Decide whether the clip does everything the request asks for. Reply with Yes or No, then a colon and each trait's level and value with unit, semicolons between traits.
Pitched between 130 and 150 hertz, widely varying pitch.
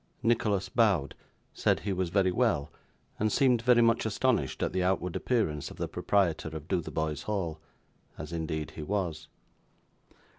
No: very low, 95 Hz; wide, 5.8 semitones